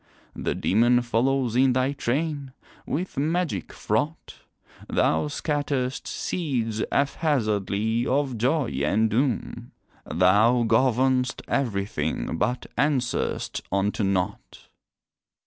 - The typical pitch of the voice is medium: No, low, 125 Hz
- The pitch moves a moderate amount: Yes, average, 4.2 semitones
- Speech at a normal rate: No, slow, 95 wpm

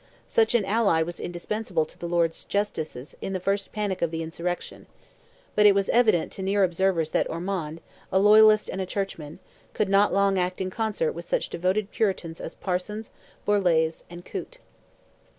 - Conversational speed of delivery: Yes, average, 175 wpm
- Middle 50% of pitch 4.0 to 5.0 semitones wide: No, average, 3.4 semitones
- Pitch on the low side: No, high, 190 Hz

